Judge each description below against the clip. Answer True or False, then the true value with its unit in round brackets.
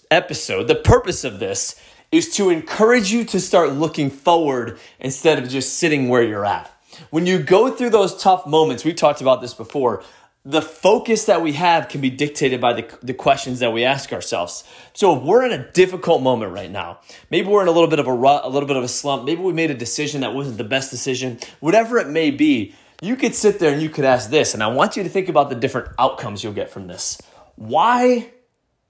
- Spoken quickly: True (230 wpm)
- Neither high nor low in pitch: True (155 Hz)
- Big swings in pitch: True (6.4 semitones)